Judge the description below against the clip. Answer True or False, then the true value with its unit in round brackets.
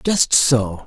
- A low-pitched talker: True (130 Hz)